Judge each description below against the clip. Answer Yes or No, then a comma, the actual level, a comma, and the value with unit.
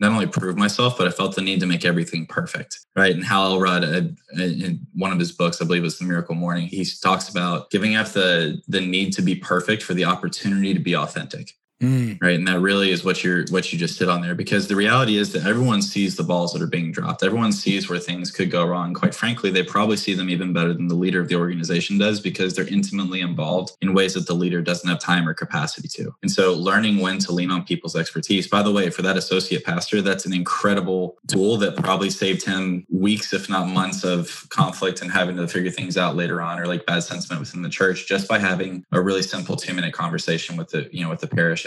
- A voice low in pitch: Yes, very low, 95 Hz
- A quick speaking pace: Yes, fast, 245 wpm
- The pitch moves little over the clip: Yes, narrow, 2.1 semitones